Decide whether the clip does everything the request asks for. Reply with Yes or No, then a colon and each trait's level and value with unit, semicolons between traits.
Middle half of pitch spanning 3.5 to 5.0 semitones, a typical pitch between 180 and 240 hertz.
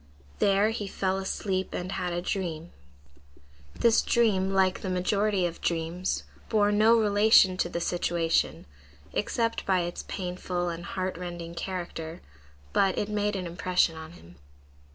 No: average, 2.7 semitones; medium, 185 Hz